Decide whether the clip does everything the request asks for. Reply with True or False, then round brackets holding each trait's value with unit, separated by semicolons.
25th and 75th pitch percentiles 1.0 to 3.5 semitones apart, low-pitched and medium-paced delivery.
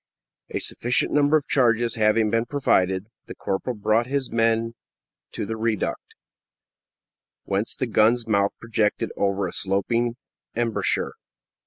False (2.4 semitones; 115 Hz; 130 wpm)